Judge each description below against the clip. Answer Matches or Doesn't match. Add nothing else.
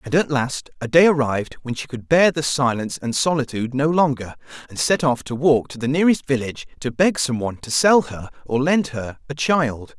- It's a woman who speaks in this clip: Doesn't match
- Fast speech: Matches